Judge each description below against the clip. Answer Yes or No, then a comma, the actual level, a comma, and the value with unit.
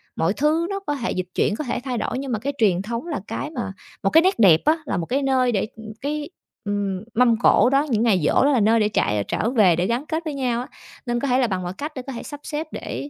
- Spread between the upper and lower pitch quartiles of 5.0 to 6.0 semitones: Yes, wide, 5.4 semitones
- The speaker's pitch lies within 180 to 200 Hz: No, high, 240 Hz